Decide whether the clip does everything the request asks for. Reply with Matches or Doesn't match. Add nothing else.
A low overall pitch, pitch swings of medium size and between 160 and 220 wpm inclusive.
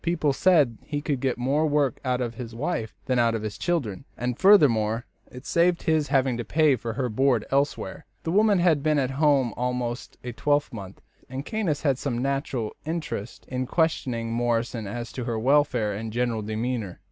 Matches